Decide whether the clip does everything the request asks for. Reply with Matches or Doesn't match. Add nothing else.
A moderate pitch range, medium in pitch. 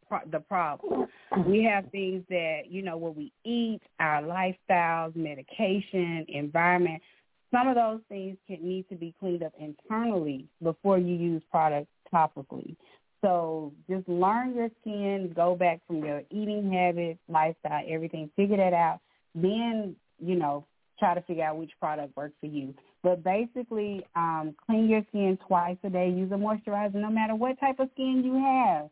Matches